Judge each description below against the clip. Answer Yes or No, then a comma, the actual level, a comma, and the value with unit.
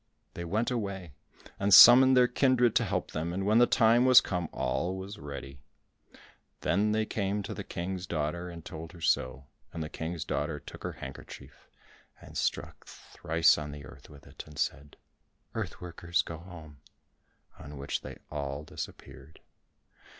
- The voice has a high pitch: No, very low, 85 Hz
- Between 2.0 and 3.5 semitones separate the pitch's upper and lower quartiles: No, average, 5.3 semitones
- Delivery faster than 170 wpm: No, average, 165 wpm